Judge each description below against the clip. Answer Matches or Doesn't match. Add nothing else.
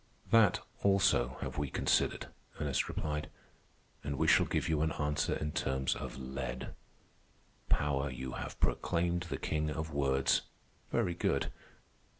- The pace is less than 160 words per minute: Matches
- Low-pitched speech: Matches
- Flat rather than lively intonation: Doesn't match